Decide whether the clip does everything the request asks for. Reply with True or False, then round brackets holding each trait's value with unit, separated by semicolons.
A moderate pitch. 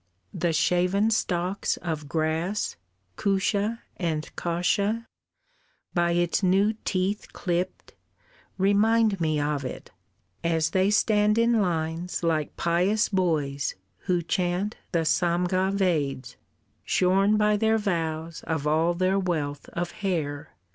True (180 Hz)